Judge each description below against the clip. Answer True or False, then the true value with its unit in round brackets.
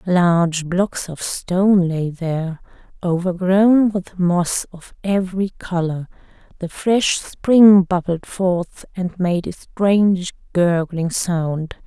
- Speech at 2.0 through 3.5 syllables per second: True (3.4 syllables/s)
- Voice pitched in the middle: True (180 Hz)